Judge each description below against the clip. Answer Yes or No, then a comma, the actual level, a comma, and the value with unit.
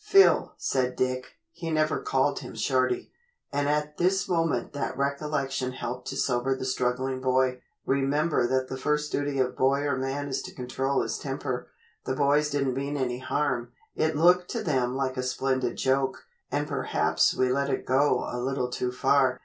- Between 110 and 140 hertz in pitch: Yes, low, 135 Hz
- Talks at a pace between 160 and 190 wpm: Yes, average, 180 wpm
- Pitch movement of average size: No, narrow, 2.3 semitones